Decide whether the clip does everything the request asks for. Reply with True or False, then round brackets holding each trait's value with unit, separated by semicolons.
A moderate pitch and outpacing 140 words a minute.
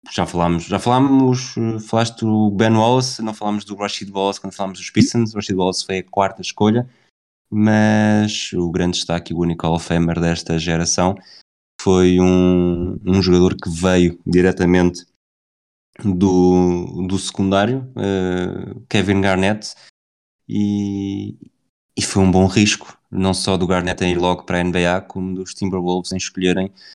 False (95 Hz; 150 wpm)